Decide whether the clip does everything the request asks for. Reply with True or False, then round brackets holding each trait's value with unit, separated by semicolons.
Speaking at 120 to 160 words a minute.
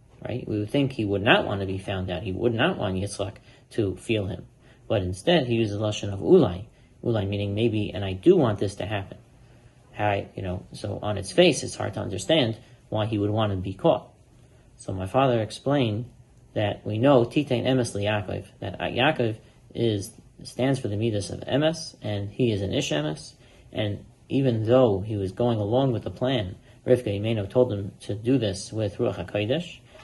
False (200 wpm)